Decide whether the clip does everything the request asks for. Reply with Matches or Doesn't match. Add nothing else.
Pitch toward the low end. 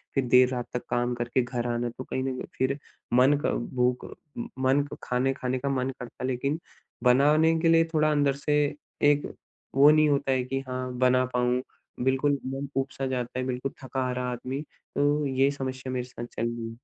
Matches